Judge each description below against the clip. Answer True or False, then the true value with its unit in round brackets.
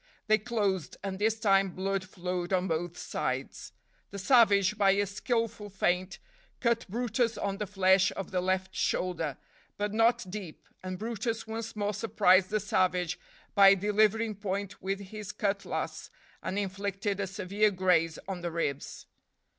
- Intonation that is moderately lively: False (2.3 semitones)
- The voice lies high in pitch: True (195 Hz)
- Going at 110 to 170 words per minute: True (150 wpm)